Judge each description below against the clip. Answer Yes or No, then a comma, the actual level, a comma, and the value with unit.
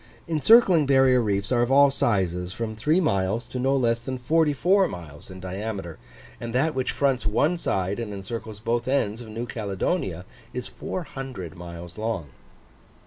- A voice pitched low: Yes, low, 115 Hz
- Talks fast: No, average, 165 wpm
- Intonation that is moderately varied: No, wide, 5.7 semitones